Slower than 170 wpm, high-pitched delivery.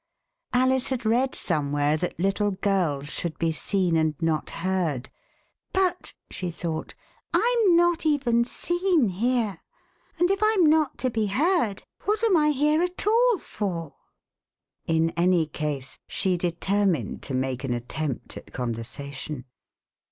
Yes: average, 140 wpm; high, 195 Hz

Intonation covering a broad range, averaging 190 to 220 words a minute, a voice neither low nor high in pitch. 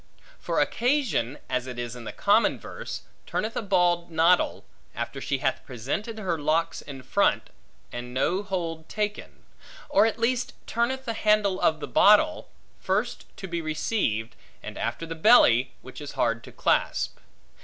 No: wide, 7.9 semitones; average, 160 wpm; medium, 175 Hz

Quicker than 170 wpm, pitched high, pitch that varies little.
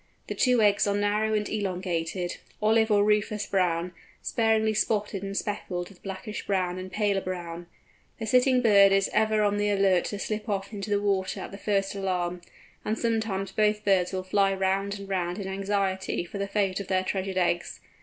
Yes: average, 190 wpm; high, 200 Hz; narrow, 2.0 semitones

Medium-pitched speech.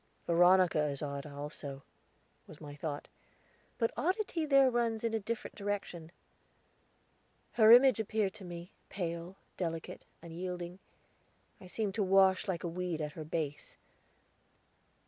Yes: medium, 180 Hz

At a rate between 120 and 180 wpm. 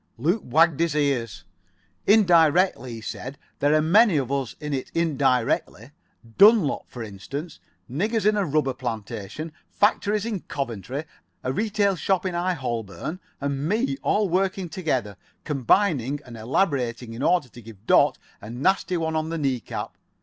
Yes: average, 155 wpm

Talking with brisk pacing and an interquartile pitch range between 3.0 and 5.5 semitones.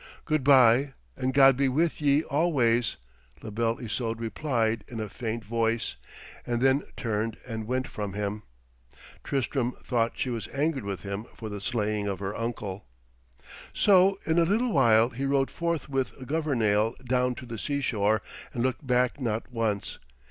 No: average, 165 wpm; average, 3.7 semitones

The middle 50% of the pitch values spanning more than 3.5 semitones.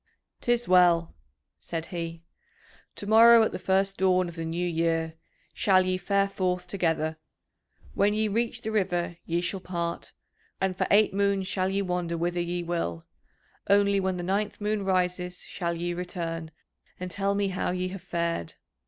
No: narrow, 2.5 semitones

